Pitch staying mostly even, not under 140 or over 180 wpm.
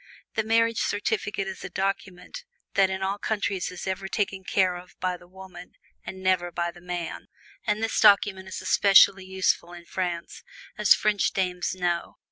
Yes: narrow, 2.1 semitones; average, 170 wpm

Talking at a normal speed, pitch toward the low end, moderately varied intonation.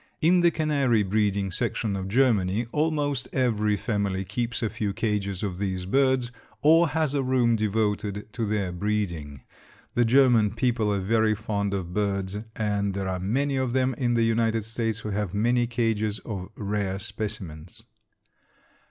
Yes: average, 160 wpm; low, 110 Hz; average, 3.5 semitones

